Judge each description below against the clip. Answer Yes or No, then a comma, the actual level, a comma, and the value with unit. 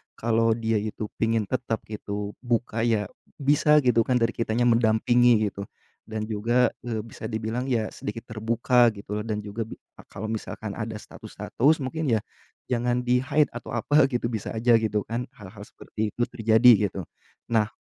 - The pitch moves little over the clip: Yes, narrow, 2.1 semitones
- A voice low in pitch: Yes, low, 115 Hz